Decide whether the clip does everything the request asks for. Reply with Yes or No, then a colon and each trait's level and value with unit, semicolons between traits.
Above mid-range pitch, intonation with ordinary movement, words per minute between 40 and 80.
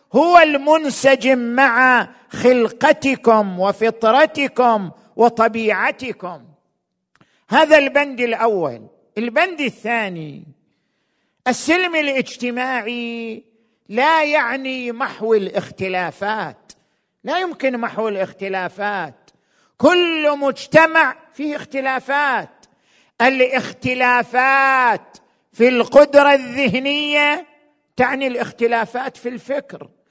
Yes: very high, 250 Hz; average, 3.9 semitones; slow, 65 wpm